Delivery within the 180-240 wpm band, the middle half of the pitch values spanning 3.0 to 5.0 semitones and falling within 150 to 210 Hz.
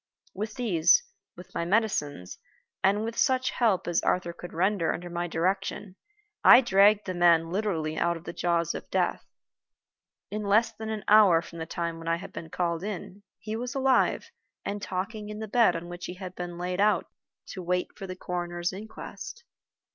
Yes: average, 185 wpm; average, 3.6 semitones; medium, 185 Hz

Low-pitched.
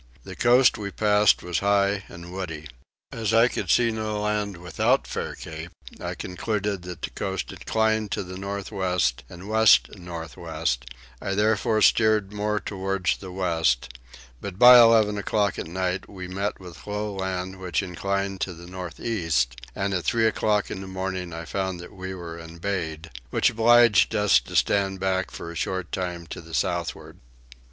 Yes: very low, 95 Hz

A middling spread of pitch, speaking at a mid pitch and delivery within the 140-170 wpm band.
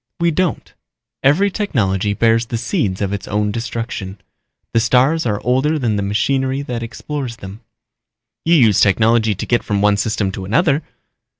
No: average, 4.7 semitones; low, 115 Hz; average, 165 wpm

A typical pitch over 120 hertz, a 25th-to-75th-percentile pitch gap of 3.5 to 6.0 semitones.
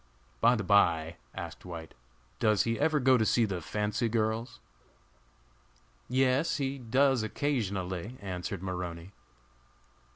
No: low, 110 Hz; wide, 5.4 semitones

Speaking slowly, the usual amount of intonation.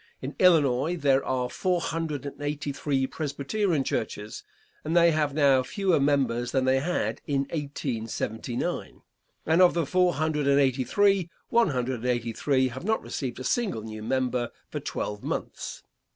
No: average, 165 wpm; average, 4.3 semitones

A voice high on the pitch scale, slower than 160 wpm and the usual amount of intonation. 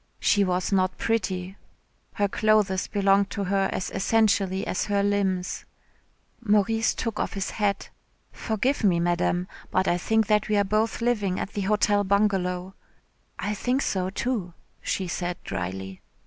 No: high, 200 Hz; average, 150 wpm; narrow, 2.3 semitones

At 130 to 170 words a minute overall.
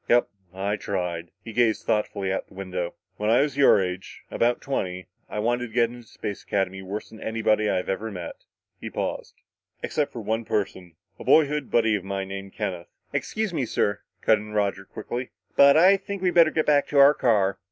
No: fast, 205 wpm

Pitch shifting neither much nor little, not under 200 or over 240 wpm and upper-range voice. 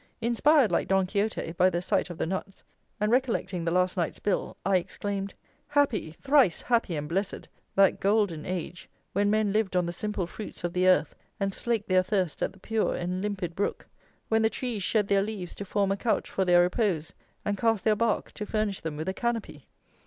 Yes: average, 3.1 semitones; fast, 205 wpm; high, 195 Hz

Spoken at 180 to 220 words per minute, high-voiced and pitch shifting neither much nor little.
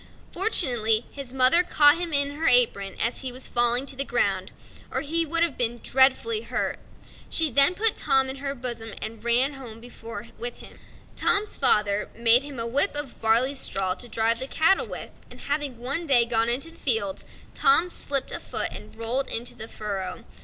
Yes: average, 190 wpm; very high, 260 Hz; average, 3.9 semitones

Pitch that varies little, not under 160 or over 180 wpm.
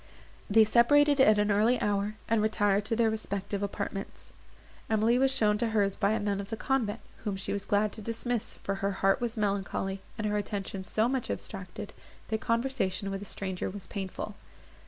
No: narrow, 2.3 semitones; average, 190 wpm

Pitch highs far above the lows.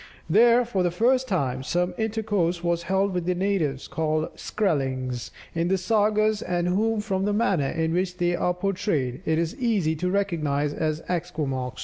No: average, 4.3 semitones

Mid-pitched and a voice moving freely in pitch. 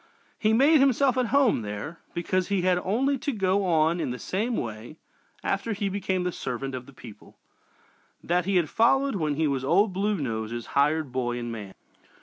Yes: medium, 180 Hz; wide, 8.2 semitones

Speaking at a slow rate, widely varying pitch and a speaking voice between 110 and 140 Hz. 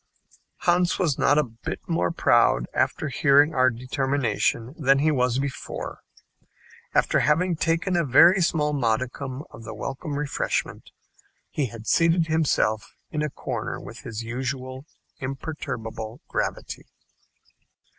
No: slow, 125 wpm; average, 3.8 semitones; low, 135 Hz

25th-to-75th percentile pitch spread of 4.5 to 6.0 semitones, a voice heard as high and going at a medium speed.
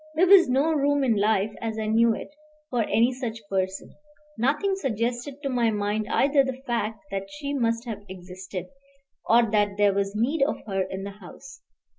Yes: average, 4.8 semitones; high, 230 Hz; average, 185 wpm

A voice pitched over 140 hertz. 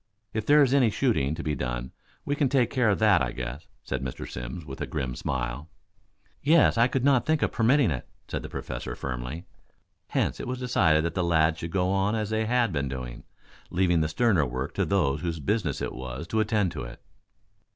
No: very low, 85 Hz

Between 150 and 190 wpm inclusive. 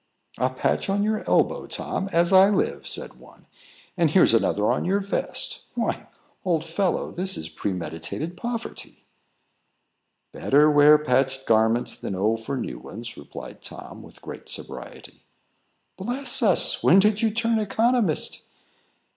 No: average, 140 wpm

